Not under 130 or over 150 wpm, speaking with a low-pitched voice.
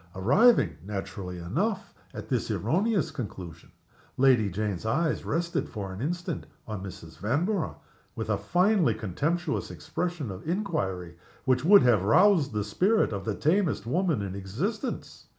Yes: average, 140 wpm; low, 125 Hz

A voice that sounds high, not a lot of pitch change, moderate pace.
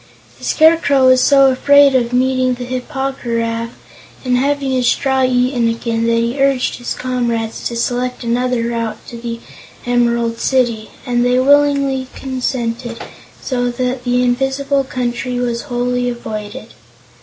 Yes: very high, 250 Hz; narrow, 1.9 semitones; average, 150 wpm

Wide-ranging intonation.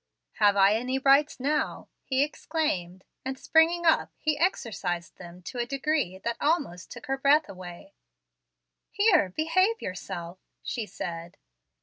Yes: wide, 8.7 semitones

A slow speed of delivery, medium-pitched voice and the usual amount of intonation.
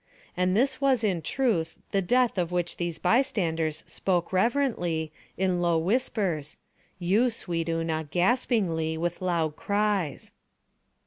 Yes: slow, 120 wpm; medium, 180 Hz; average, 5.0 semitones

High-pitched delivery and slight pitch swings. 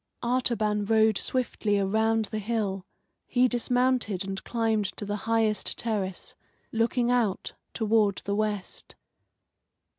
Yes: high, 220 Hz; narrow, 2.3 semitones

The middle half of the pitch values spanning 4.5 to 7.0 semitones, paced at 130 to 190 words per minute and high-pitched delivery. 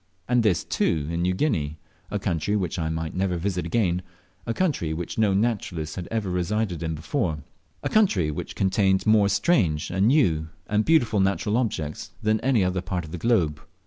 No: average, 4.9 semitones; average, 185 wpm; very low, 95 Hz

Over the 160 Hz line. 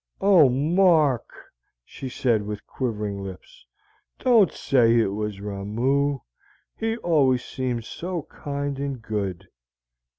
No: low, 130 Hz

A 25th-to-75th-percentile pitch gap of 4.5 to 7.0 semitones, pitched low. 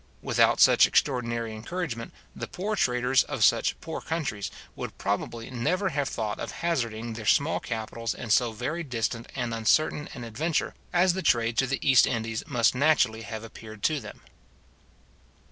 Yes: average, 4.8 semitones; low, 120 Hz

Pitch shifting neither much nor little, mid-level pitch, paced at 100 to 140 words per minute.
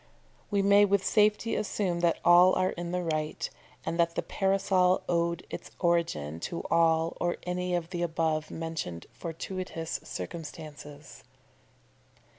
No: narrow, 2.2 semitones; medium, 170 Hz; slow, 135 wpm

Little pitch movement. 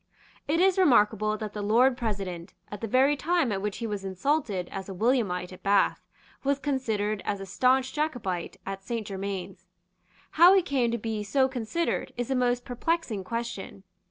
No: average, 5.0 semitones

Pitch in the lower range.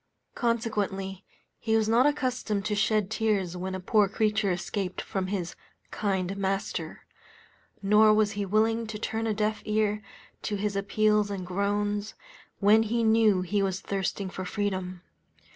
No: high, 205 Hz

